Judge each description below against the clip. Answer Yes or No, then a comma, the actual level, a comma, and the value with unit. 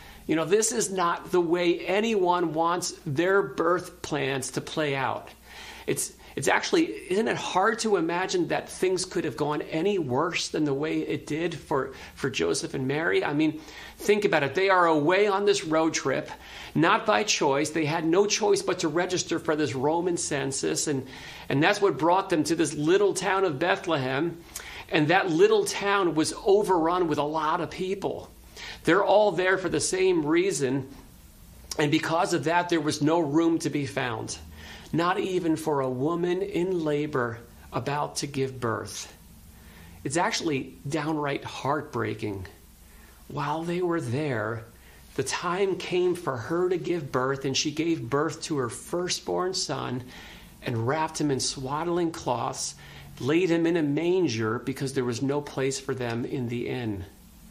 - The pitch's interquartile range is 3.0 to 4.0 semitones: No, average, 4.9 semitones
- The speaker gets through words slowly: No, average, 170 wpm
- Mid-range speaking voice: Yes, medium, 160 Hz